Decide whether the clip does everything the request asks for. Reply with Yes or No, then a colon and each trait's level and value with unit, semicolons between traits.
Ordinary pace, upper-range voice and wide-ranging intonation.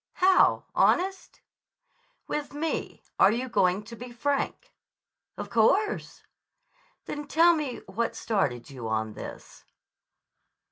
No: slow, 110 wpm; high, 245 Hz; wide, 8.6 semitones